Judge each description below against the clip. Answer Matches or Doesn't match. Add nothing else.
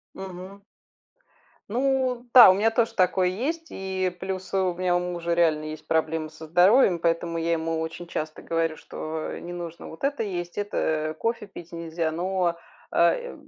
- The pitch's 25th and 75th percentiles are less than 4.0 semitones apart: Matches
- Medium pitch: Matches